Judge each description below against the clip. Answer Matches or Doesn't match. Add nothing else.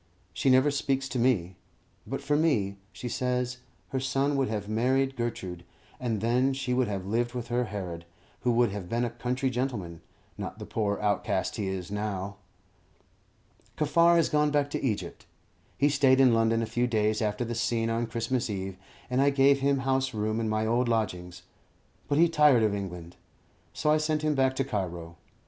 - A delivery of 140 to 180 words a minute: Doesn't match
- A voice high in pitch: Doesn't match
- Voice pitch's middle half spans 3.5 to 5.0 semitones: Matches